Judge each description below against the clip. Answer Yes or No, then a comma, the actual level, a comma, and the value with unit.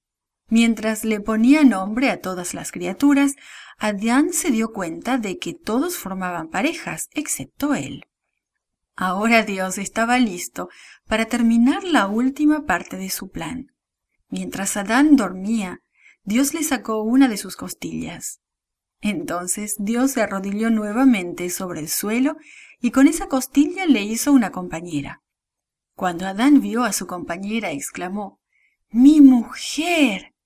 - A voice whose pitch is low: No, high, 225 Hz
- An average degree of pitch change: No, wide, 5.7 semitones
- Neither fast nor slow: No, slow, 130 wpm